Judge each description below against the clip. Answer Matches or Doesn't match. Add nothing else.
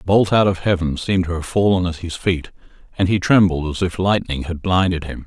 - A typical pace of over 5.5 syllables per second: Matches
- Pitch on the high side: Doesn't match